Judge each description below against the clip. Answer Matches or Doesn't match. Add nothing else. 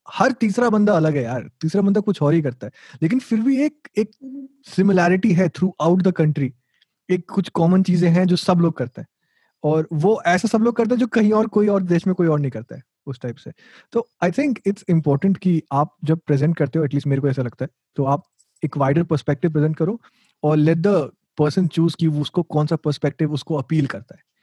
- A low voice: Doesn't match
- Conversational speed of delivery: Doesn't match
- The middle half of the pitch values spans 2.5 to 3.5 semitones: Doesn't match